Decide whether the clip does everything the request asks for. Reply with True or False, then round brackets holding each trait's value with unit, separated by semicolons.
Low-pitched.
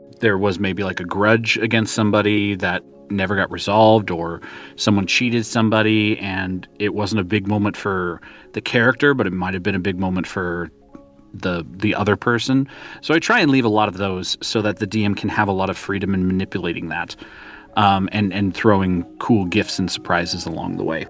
True (100 Hz)